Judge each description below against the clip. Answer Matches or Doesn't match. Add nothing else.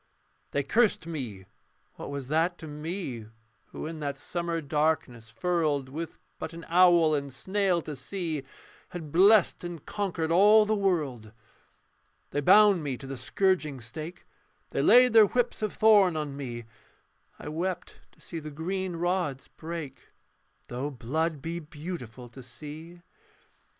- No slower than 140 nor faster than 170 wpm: Matches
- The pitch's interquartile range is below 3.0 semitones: Doesn't match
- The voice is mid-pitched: Matches